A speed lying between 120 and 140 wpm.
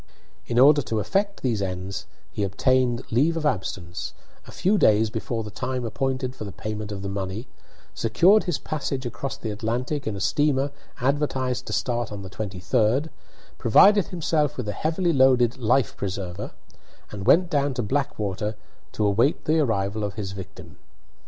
No: average, 165 wpm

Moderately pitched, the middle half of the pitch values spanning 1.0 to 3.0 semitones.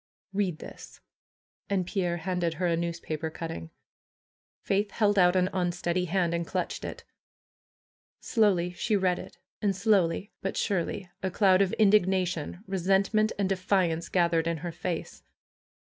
Yes: medium, 180 Hz; narrow, 2.4 semitones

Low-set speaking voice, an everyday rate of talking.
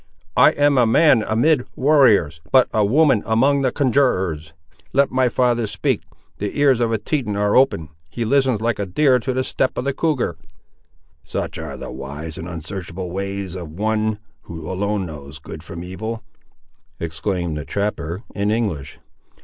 Yes: low, 105 Hz; average, 165 wpm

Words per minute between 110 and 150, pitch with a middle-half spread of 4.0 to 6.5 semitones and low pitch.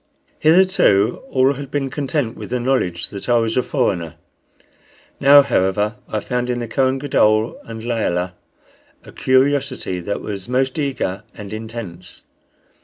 Yes: average, 145 wpm; average, 4.6 semitones; low, 120 Hz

